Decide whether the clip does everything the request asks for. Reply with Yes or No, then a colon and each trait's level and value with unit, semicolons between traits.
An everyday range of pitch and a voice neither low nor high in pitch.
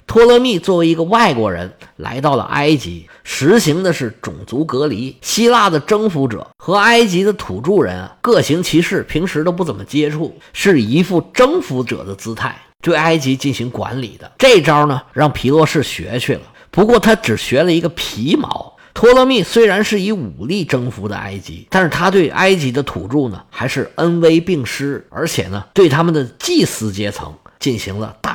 No: wide, 7.7 semitones; medium, 150 Hz